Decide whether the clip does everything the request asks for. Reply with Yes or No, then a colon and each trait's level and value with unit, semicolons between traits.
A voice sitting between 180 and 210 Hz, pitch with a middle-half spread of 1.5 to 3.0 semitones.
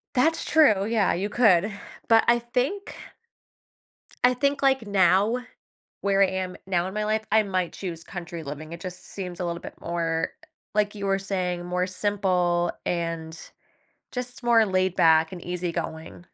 No: high, 190 Hz; average, 3.9 semitones